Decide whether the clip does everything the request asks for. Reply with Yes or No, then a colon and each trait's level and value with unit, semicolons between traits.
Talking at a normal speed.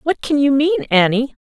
No: fast, 210 wpm